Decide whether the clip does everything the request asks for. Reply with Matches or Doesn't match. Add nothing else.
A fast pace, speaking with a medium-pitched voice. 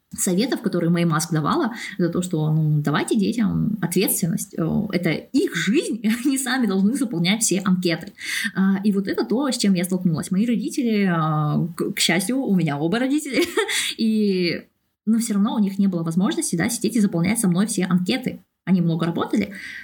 Doesn't match